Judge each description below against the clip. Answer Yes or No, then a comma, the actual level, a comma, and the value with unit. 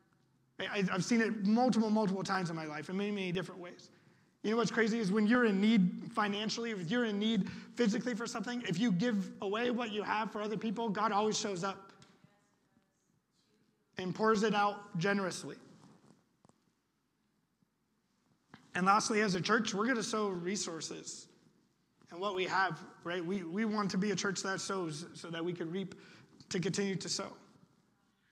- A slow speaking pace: No, average, 175 wpm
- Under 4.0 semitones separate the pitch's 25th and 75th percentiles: Yes, average, 2.8 semitones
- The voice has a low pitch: No, high, 200 Hz